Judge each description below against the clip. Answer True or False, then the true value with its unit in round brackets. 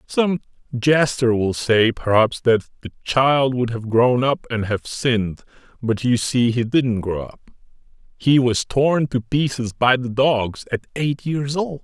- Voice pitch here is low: True (125 Hz)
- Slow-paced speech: False (170 wpm)